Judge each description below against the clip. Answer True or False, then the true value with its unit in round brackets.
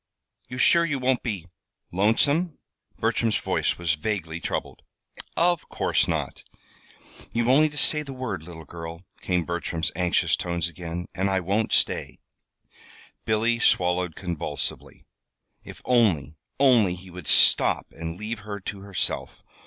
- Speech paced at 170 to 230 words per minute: False (135 wpm)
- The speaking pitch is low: True (95 Hz)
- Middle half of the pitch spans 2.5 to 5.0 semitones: False (5.5 semitones)